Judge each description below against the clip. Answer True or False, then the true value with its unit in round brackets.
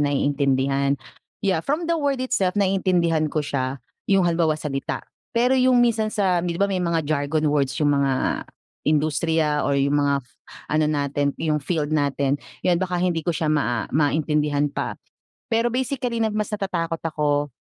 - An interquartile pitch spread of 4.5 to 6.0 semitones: True (4.8 semitones)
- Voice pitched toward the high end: False (155 Hz)